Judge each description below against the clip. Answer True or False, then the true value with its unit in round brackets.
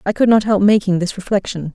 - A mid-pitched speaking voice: False (200 Hz)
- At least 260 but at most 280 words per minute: False (240 wpm)